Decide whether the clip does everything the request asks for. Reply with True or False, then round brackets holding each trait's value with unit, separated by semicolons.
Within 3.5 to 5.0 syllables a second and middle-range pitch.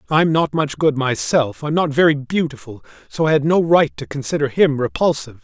False (5.4 syllables/s; 145 Hz)